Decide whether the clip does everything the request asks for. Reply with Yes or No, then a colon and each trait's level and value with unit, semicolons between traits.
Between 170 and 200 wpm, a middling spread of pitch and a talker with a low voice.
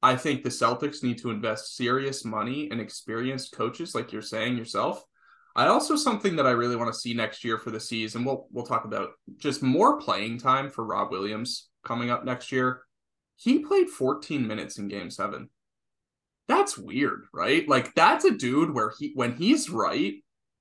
Yes: average, 185 wpm; average, 3.8 semitones; low, 125 Hz